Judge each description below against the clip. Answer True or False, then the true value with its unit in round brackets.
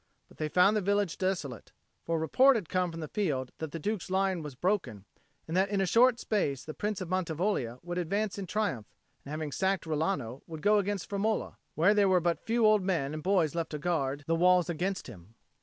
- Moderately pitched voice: True (180 Hz)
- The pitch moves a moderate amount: True (4.4 semitones)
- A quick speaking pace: True (225 wpm)